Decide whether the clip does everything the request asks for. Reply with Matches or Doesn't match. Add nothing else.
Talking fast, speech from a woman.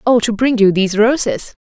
Matches